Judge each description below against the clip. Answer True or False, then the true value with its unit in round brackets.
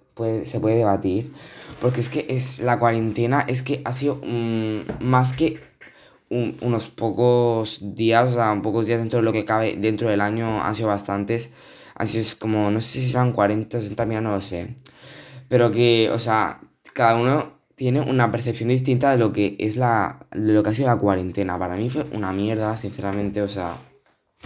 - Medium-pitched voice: False (115 Hz)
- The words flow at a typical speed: False (195 wpm)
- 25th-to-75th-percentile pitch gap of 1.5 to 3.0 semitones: True (2.5 semitones)